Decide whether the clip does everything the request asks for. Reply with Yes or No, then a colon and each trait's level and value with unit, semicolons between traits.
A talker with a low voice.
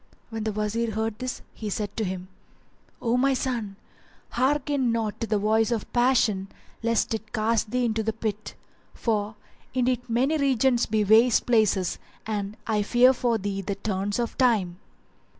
No: high, 225 Hz